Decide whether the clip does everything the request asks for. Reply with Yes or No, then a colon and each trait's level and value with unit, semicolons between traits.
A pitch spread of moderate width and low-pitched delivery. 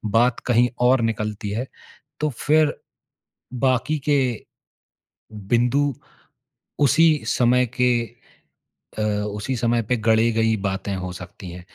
Yes: average, 3.6 semitones; low, 120 Hz